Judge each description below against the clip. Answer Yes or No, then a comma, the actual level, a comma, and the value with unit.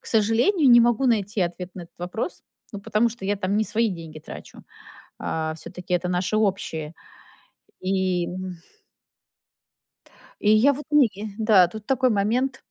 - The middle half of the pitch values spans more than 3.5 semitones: Yes, average, 4.2 semitones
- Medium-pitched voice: No, high, 205 Hz